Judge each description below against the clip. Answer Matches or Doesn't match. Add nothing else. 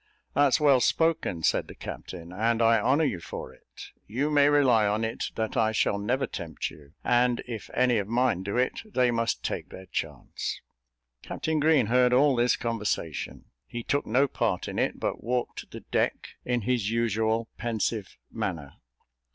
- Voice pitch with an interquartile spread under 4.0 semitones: Matches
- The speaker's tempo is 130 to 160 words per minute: Doesn't match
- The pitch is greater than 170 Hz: Doesn't match